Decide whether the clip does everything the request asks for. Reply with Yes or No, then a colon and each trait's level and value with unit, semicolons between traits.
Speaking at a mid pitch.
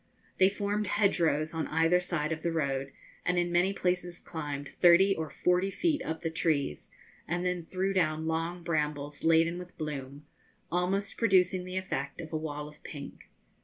Yes: medium, 170 Hz